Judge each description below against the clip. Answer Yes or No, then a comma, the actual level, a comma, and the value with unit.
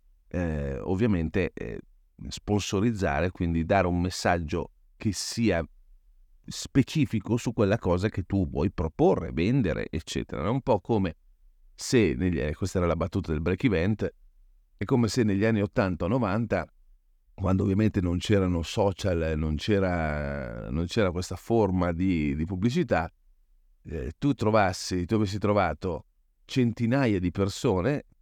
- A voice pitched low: Yes, very low, 95 Hz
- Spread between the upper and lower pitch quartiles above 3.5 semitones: Yes, average, 4.1 semitones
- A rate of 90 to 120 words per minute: No, average, 135 wpm